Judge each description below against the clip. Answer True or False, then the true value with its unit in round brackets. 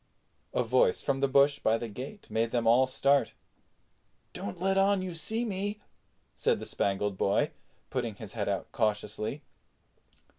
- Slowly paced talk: False (155 wpm)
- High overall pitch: False (130 Hz)